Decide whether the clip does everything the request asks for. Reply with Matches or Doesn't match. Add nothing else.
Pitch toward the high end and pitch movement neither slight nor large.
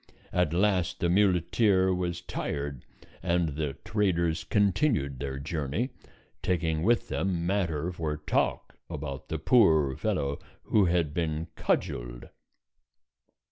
Doesn't match